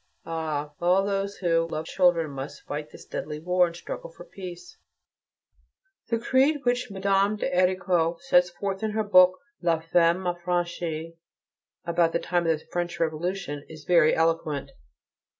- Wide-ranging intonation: No, average, 2.7 semitones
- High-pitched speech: No, medium, 175 Hz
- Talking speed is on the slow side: No, average, 155 wpm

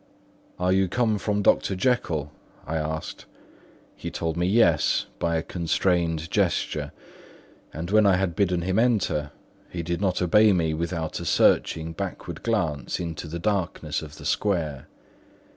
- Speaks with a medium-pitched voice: No, very low, 85 Hz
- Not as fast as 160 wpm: Yes, average, 150 wpm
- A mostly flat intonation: No, average, 3.4 semitones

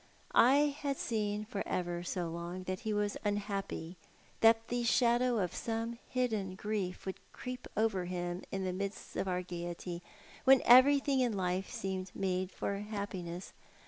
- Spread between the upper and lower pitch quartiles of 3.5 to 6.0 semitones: Yes, average, 4.1 semitones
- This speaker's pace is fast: No, average, 160 wpm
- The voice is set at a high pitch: Yes, high, 200 Hz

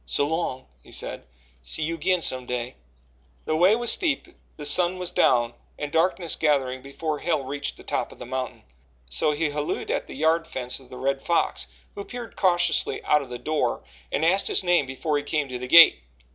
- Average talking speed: No, fast, 210 wpm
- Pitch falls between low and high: Yes, medium, 150 Hz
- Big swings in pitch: No, average, 4.6 semitones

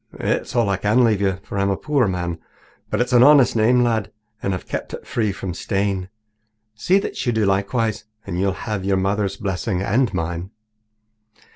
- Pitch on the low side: Yes, low, 100 Hz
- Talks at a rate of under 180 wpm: No, average, 190 wpm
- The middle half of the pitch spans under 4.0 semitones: Yes, average, 3.4 semitones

